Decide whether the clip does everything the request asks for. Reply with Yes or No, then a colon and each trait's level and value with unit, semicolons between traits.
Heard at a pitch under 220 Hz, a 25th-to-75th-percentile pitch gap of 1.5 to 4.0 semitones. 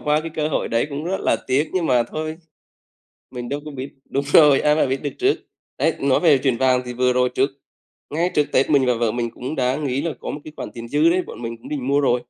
Yes: medium, 140 Hz; average, 3.3 semitones